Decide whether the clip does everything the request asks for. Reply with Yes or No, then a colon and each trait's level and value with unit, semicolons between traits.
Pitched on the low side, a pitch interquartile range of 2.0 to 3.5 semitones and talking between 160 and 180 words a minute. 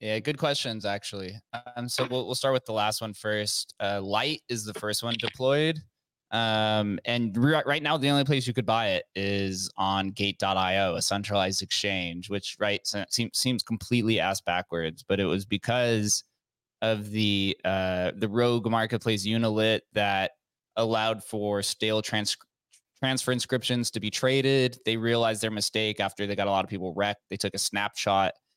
Yes: low, 110 Hz; average, 3.1 semitones; average, 175 wpm